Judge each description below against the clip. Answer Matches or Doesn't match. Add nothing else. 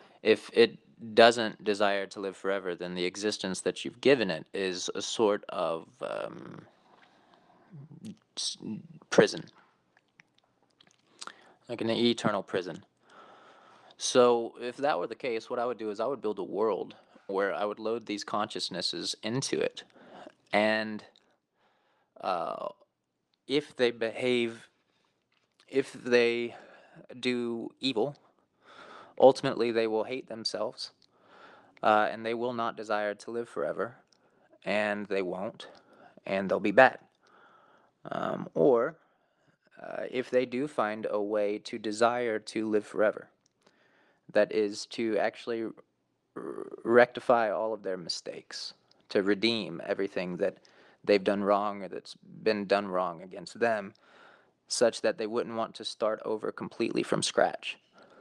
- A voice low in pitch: Matches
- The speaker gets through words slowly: Matches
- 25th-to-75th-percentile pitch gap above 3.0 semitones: Doesn't match